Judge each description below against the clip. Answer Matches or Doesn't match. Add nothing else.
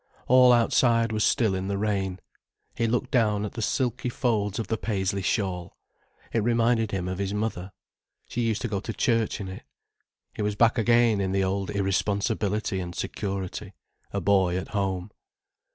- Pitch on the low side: Matches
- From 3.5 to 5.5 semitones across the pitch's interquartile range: Doesn't match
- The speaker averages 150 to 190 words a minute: Matches